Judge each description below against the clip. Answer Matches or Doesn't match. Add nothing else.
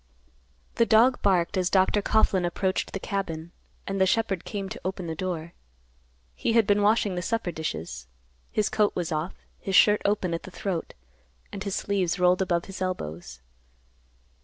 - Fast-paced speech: Doesn't match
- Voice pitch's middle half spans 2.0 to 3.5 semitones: Matches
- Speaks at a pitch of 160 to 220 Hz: Matches